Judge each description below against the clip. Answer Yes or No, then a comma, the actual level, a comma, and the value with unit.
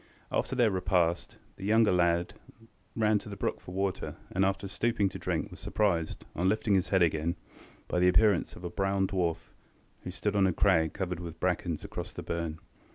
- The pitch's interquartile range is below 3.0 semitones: Yes, narrow, 2.5 semitones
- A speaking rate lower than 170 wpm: No, average, 195 wpm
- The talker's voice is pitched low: Yes, very low, 95 Hz